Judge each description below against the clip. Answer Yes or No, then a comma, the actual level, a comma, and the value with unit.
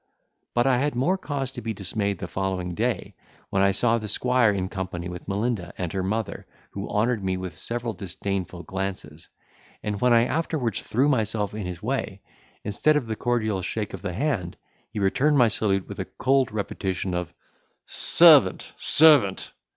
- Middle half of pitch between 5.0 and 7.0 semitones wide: No, average, 4.3 semitones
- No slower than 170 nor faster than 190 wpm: Yes, average, 175 wpm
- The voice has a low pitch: Yes, low, 105 Hz